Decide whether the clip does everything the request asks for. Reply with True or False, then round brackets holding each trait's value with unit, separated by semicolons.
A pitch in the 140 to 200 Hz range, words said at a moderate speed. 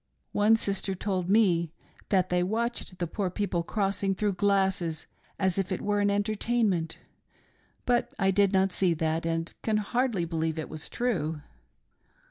True (190 Hz; 155 wpm)